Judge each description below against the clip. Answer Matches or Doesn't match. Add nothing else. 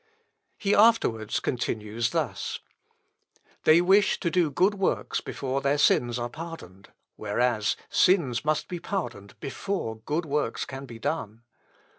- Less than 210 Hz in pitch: Matches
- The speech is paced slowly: Matches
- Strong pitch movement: Matches